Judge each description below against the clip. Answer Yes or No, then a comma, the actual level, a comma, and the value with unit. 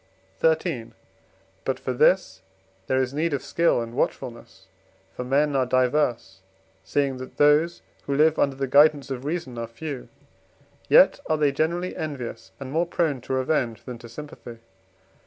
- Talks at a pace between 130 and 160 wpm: Yes, average, 155 wpm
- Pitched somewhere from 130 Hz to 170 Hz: Yes, medium, 140 Hz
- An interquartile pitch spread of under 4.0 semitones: Yes, average, 3.5 semitones